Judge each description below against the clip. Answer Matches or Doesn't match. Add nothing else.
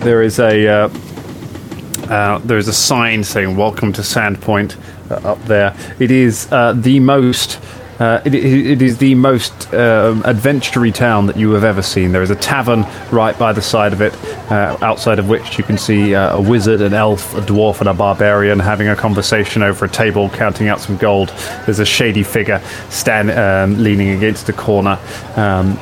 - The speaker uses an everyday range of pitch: Doesn't match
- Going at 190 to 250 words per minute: Matches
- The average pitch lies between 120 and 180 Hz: Doesn't match